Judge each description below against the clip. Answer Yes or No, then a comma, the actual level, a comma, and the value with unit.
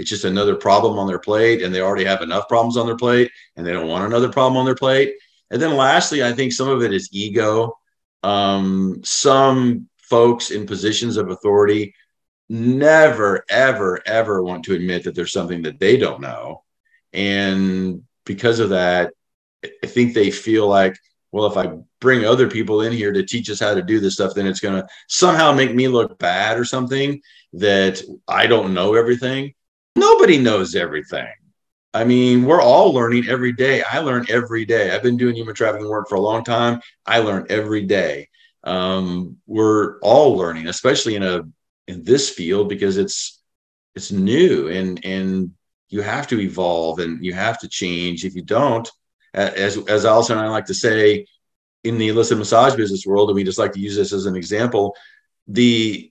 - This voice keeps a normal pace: Yes, average, 190 wpm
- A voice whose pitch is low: Yes, low, 110 Hz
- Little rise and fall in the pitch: No, average, 4.1 semitones